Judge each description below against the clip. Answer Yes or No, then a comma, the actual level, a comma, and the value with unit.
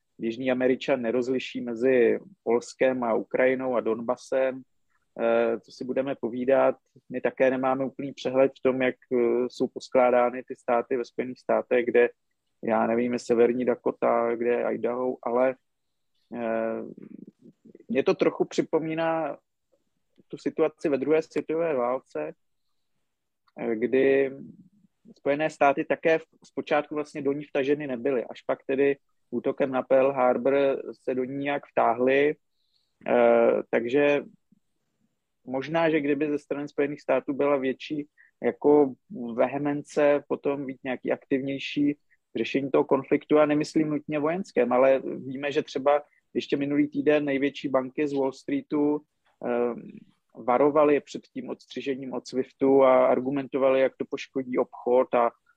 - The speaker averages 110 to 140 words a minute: Yes, average, 130 wpm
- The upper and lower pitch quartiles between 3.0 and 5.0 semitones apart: No, narrow, 2.6 semitones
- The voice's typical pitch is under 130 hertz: No, low, 135 Hz